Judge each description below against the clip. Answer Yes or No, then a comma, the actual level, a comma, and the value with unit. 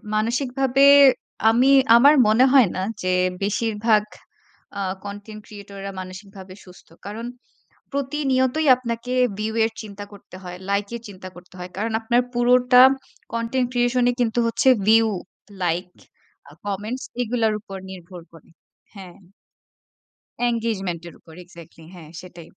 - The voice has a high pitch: Yes, high, 215 Hz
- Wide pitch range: No, average, 4.3 semitones